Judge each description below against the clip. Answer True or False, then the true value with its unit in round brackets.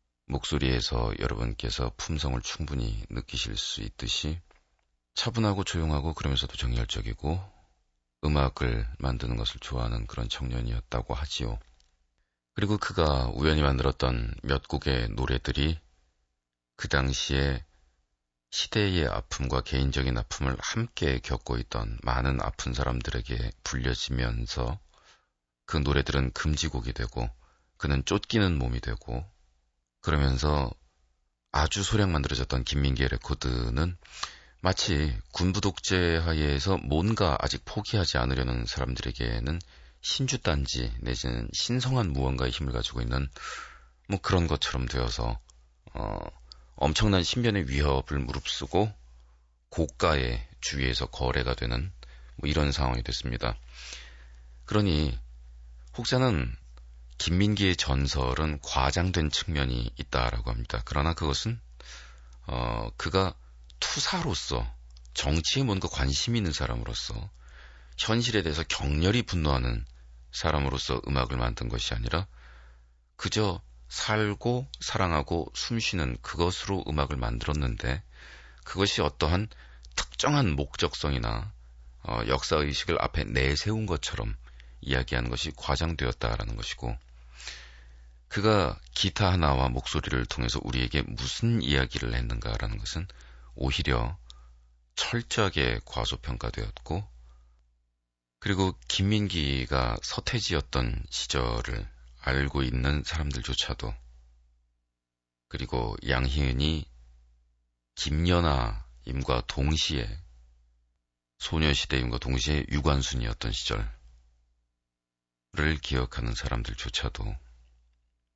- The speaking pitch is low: True (65 Hz)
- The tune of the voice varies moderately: True (4.7 semitones)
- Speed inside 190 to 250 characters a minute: False (260 characters per minute)